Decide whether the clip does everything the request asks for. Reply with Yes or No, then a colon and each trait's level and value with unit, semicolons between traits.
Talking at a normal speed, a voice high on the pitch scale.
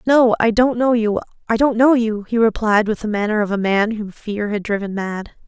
No: fast, 230 wpm; high, 220 Hz